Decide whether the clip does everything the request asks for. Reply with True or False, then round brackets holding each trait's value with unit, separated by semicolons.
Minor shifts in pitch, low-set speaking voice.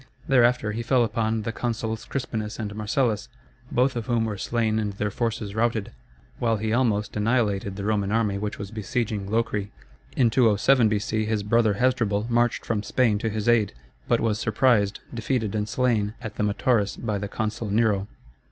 True (2.1 semitones; 110 Hz)